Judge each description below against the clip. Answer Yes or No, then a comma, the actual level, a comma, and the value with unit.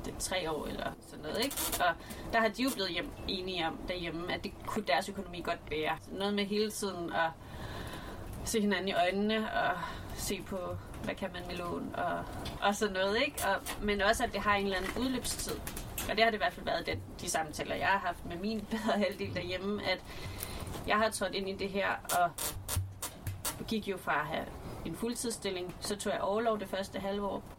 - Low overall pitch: No, high, 195 Hz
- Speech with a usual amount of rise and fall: Yes, average, 3.6 semitones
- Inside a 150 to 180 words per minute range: No, average, 215 wpm